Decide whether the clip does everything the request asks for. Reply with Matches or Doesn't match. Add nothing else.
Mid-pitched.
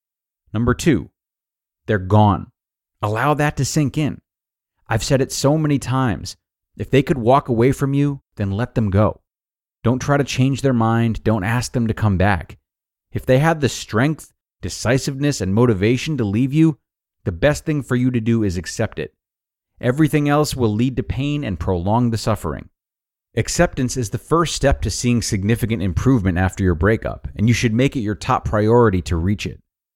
Doesn't match